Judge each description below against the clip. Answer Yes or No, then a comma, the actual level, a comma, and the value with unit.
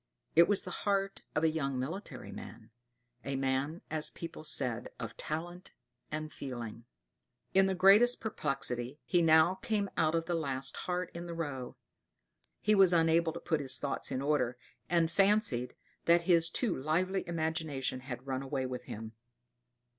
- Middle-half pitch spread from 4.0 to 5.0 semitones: Yes, average, 4.7 semitones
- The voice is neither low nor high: Yes, medium, 160 Hz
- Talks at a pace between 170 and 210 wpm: No, average, 160 wpm